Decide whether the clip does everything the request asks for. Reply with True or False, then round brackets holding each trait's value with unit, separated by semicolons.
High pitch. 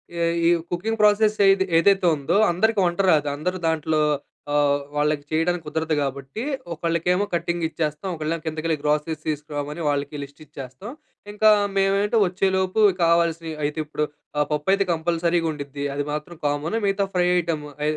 False (165 Hz)